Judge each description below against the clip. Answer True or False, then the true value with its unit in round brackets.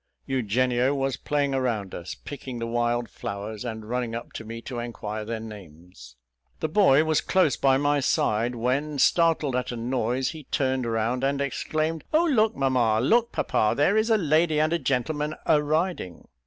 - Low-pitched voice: True (130 Hz)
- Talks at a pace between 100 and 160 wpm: False (180 wpm)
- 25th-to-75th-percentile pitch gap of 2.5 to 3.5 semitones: False (4.7 semitones)